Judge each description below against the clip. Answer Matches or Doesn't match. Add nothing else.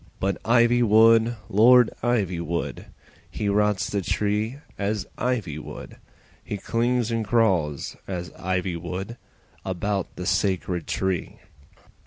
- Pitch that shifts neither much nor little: Matches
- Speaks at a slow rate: Matches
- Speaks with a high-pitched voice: Doesn't match